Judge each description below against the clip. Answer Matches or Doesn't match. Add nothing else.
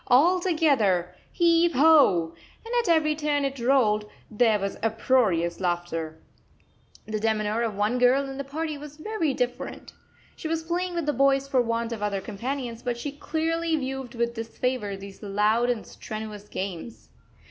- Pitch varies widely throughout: Matches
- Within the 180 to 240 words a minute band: Doesn't match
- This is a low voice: Doesn't match